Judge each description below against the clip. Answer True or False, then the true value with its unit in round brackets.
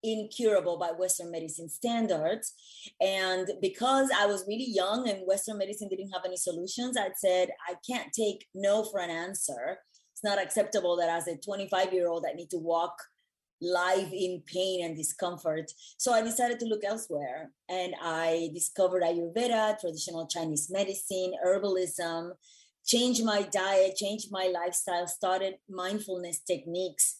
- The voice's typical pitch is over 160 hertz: True (185 Hz)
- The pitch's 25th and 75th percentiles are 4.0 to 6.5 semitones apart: False (2.7 semitones)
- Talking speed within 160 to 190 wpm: False (150 wpm)